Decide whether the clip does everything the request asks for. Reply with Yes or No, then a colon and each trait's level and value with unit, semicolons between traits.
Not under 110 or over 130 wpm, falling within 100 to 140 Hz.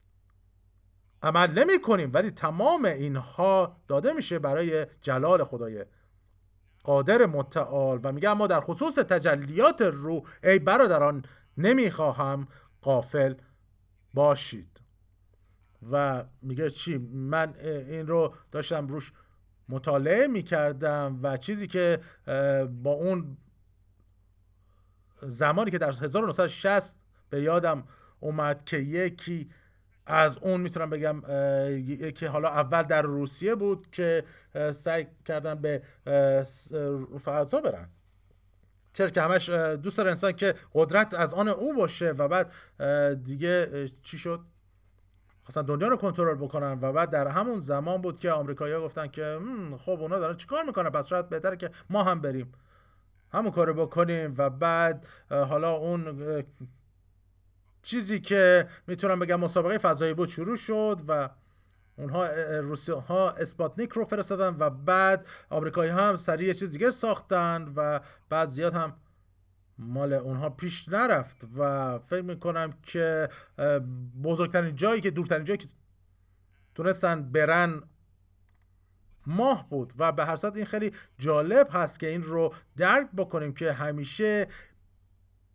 No: average, 125 wpm; medium, 155 Hz